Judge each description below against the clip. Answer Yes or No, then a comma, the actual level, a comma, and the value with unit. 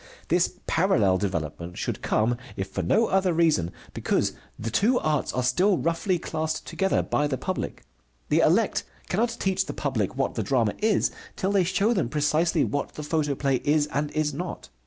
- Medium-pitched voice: Yes, medium, 155 Hz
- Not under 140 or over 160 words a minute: No, average, 180 wpm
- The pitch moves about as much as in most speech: No, wide, 6.4 semitones